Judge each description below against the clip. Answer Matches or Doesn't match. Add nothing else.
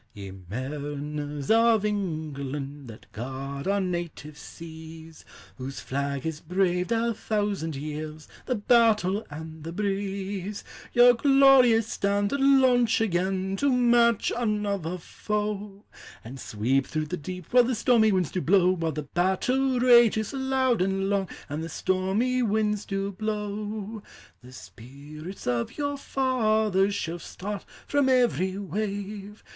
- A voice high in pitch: Matches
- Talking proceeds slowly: Matches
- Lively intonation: Matches